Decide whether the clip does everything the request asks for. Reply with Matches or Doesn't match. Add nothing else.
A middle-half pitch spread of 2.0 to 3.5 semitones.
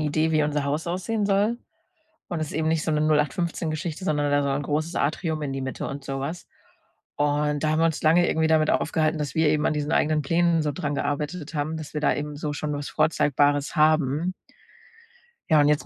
Doesn't match